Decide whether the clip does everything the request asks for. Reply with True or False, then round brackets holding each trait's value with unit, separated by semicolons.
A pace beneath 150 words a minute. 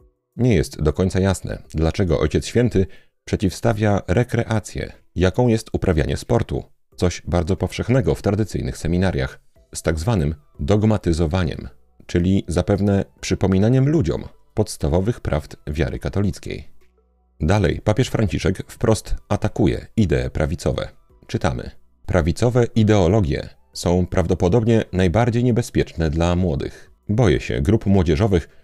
True (110 wpm)